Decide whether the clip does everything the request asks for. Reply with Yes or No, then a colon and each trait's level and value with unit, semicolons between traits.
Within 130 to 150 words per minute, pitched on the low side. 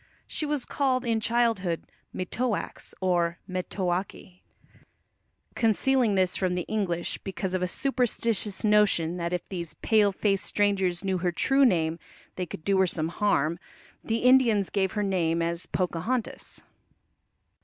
No: average, 140 wpm; high, 190 Hz